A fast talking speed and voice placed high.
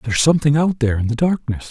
No: fast, 280 wpm; medium, 140 Hz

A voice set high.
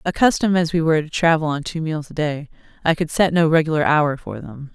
No: medium, 155 Hz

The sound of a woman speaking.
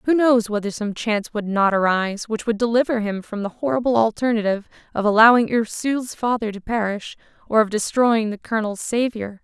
Yes: female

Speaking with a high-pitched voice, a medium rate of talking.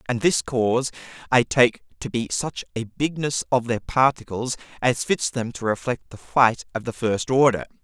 No: low, 125 Hz; average, 185 wpm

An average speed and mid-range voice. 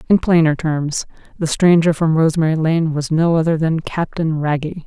Yes: average, 160 wpm; medium, 160 Hz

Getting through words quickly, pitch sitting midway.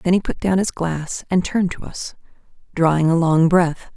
Yes: fast, 210 wpm; medium, 170 Hz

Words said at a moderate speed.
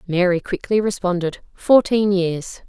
No: slow, 110 wpm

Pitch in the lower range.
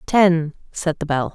No: medium, 165 Hz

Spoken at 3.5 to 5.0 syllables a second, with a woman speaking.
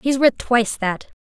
Yes: 4.6 syllables/s; female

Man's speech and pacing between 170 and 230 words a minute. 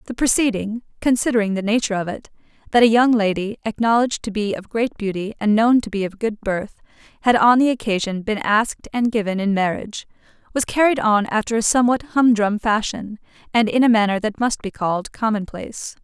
No: female; average, 185 wpm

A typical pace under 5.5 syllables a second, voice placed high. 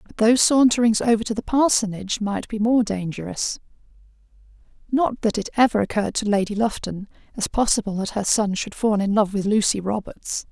No: 5.7 syllables/s; high, 215 Hz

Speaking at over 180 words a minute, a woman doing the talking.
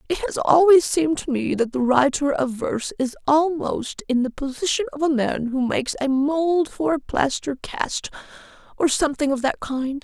Yes: average, 190 wpm; female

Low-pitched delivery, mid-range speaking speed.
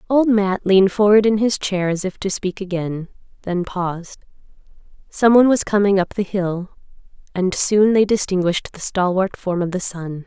No: high, 195 Hz; average, 175 wpm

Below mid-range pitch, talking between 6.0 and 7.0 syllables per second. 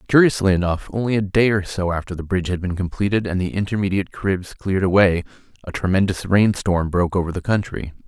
Yes: very low, 95 Hz; 6.2 syllables/s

